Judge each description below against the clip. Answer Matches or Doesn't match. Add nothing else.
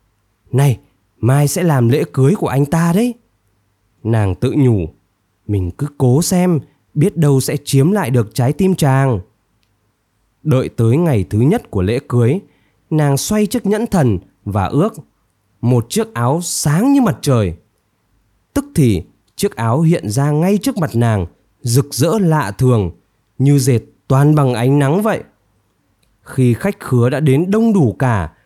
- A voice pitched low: Matches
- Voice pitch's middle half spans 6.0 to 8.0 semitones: Matches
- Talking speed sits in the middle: Doesn't match